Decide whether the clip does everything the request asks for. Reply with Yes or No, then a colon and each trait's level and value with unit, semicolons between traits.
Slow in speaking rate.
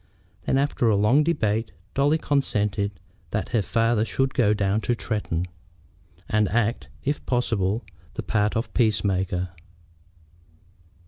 Yes: slow, 130 wpm